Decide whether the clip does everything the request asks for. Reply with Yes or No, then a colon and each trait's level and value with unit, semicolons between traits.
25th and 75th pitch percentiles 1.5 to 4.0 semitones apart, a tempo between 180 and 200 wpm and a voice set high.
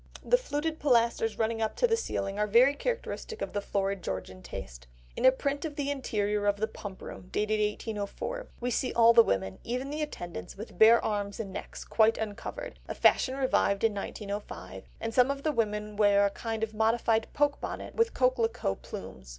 No: average, 4.4 semitones; average, 190 wpm; high, 225 Hz